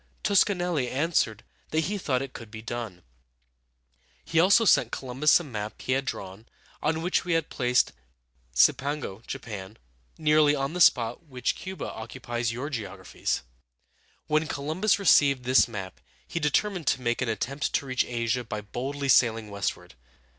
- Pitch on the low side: Yes, low, 130 Hz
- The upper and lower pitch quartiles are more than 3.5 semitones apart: Yes, average, 5.1 semitones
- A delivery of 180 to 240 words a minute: No, average, 155 wpm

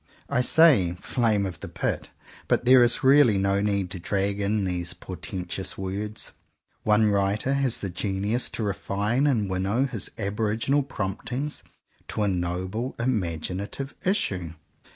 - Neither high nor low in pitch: No, low, 105 Hz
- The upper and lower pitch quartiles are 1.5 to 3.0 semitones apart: No, average, 4.2 semitones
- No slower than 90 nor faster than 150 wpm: Yes, average, 140 wpm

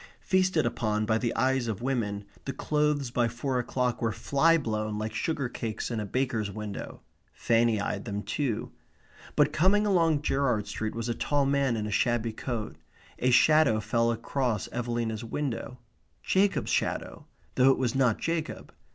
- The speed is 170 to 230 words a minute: No, average, 160 wpm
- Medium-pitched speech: No, low, 120 Hz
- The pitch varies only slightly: No, average, 4.0 semitones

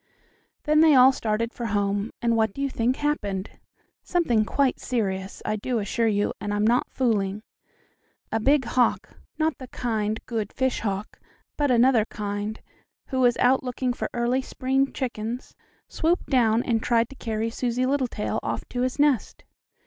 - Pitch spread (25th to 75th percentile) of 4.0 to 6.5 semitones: No, average, 3.3 semitones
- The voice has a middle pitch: No, high, 235 Hz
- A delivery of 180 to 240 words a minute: No, average, 165 wpm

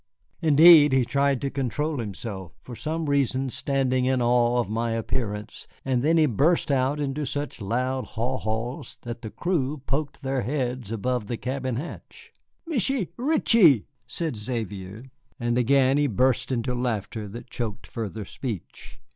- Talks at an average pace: Yes, average, 155 wpm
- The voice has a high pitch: No, low, 130 Hz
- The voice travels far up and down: No, average, 3.5 semitones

